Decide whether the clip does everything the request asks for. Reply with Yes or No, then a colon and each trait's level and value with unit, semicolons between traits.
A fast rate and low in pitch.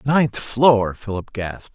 No: slow, 135 wpm; low, 115 Hz